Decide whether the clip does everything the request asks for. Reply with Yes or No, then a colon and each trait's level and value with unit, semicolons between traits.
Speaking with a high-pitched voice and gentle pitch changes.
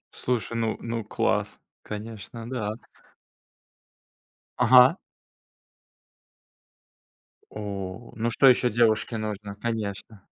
No: low, 110 Hz; narrow, 2.1 semitones